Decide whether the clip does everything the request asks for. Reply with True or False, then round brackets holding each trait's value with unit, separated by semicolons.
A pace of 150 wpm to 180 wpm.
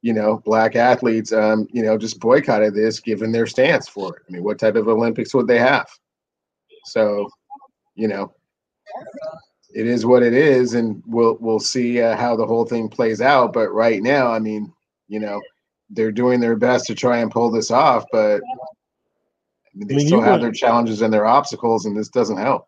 False (195 wpm)